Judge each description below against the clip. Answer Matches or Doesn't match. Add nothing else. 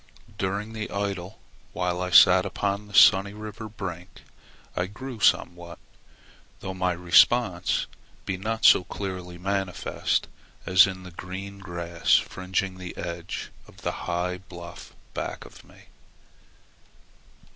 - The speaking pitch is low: Matches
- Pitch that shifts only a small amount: Matches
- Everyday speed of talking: Doesn't match